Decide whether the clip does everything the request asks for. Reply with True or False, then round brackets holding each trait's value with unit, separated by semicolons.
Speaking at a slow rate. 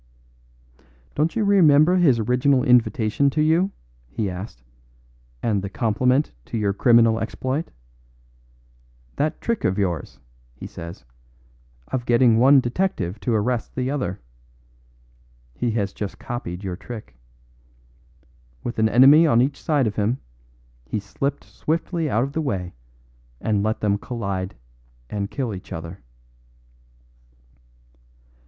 True (125 wpm)